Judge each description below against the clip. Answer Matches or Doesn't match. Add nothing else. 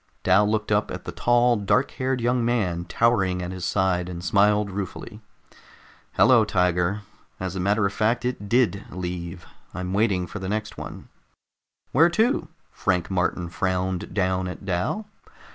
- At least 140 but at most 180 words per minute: Matches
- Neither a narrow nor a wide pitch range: Matches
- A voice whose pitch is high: Doesn't match